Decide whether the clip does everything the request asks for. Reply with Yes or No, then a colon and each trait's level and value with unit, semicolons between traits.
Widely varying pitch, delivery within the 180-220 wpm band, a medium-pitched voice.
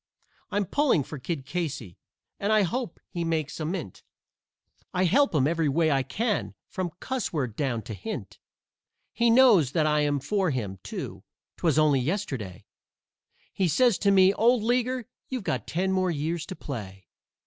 No: wide, 6.6 semitones; average, 165 wpm; medium, 165 Hz